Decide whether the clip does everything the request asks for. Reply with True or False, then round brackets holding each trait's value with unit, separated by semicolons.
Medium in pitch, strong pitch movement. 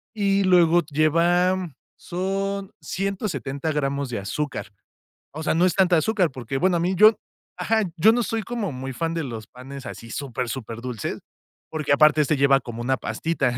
True (160 Hz; 5.7 semitones)